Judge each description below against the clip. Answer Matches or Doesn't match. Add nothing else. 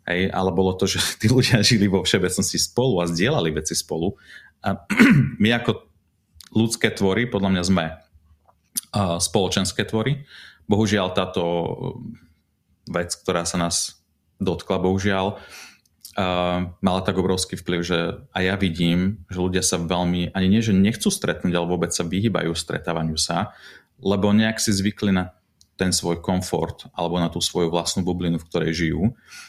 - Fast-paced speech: Doesn't match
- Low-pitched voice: Matches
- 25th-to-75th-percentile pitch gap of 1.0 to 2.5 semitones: Doesn't match